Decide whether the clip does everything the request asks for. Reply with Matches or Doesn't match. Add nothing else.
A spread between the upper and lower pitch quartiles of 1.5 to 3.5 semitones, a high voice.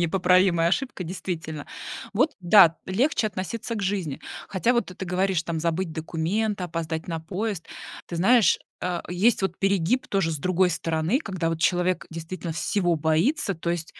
Doesn't match